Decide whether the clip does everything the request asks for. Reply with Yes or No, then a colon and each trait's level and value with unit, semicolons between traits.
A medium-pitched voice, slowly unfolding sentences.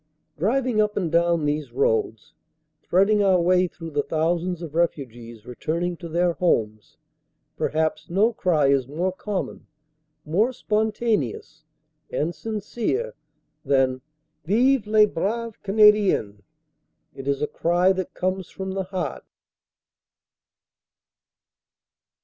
Yes: medium, 175 Hz; slow, 115 wpm